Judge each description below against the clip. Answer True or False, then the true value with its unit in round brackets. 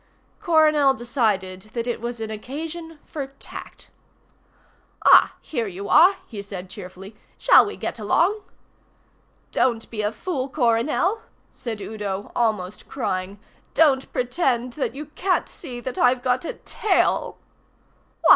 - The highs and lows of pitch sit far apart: True (6.0 semitones)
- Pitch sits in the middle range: False (240 Hz)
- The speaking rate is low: True (130 wpm)